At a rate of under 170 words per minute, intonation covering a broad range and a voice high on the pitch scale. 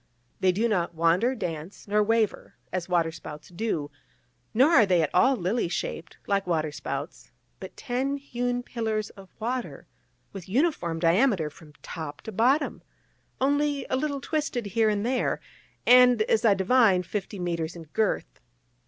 Yes: average, 150 wpm; wide, 6.1 semitones; high, 210 Hz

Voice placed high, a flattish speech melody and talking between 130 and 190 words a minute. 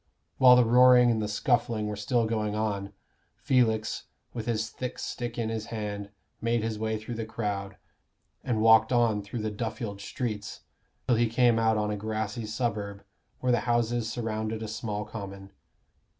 No: low, 110 Hz; narrow, 1.9 semitones; average, 170 wpm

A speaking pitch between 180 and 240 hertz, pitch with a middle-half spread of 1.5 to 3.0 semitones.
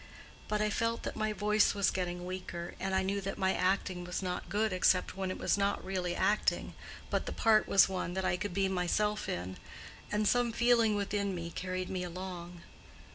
Yes: high, 190 Hz; narrow, 2.4 semitones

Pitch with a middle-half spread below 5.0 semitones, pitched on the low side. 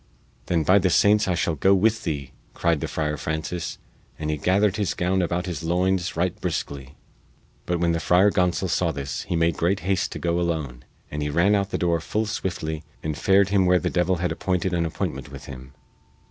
Yes: average, 3.0 semitones; very low, 85 Hz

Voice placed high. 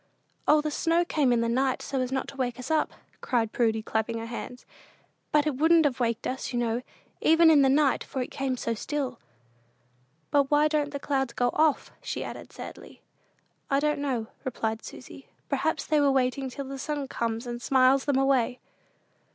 Yes: very high, 265 Hz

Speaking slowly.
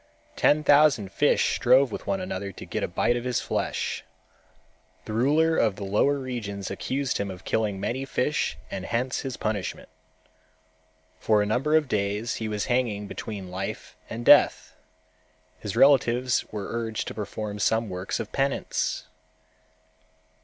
No: average, 155 wpm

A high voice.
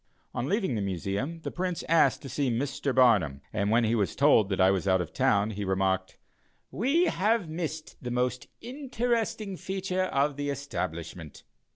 No: low, 130 Hz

